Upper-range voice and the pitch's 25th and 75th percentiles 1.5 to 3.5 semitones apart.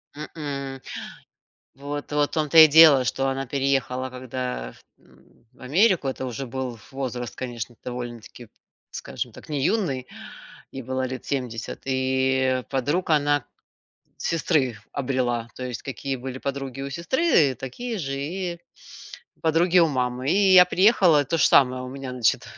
No: low, 135 Hz; average, 3.0 semitones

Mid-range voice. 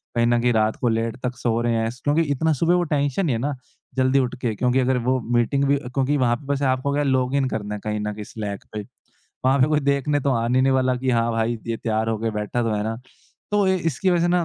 No: low, 125 Hz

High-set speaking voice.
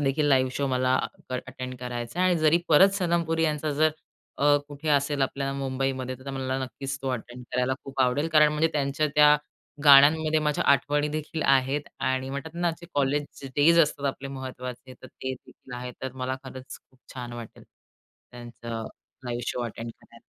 No: low, 135 Hz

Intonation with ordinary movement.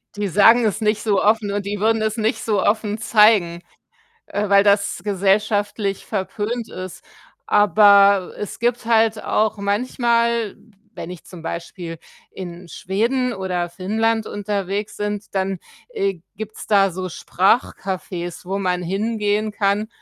No: narrow, 2.3 semitones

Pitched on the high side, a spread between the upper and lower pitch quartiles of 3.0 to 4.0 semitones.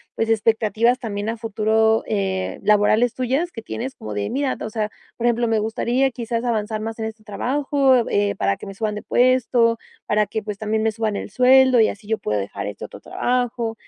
No: high, 225 Hz; narrow, 2.5 semitones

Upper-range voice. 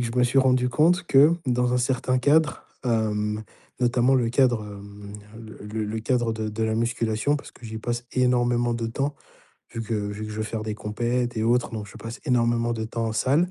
No: low, 120 Hz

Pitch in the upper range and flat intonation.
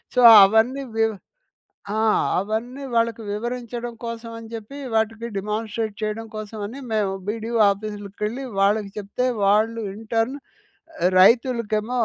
Yes: high, 225 Hz; narrow, 1.8 semitones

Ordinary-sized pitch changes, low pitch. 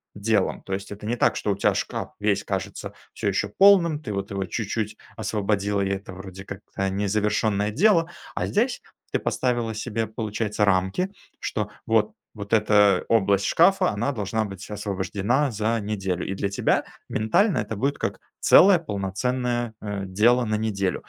Yes: average, 3.1 semitones; low, 105 Hz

